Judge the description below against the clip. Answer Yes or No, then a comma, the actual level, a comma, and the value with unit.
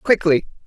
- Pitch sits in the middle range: Yes, medium, 165 Hz